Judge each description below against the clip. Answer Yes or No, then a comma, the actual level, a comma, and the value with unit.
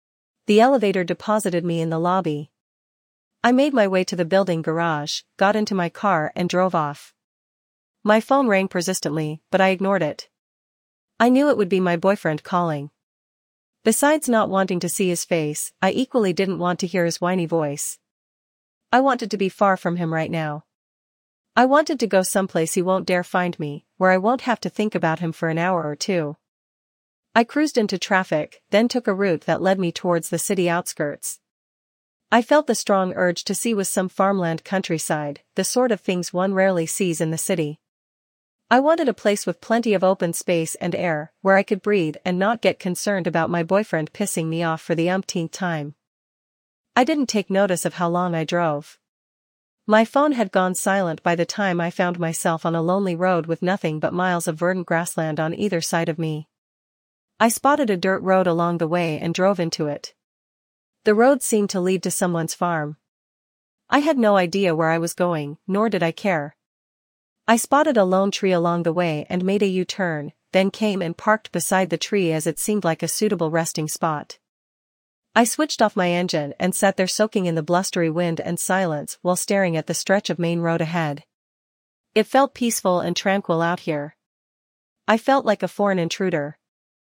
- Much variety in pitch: No, average, 3.3 semitones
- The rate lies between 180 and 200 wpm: Yes, average, 195 wpm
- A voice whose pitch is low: No, medium, 180 Hz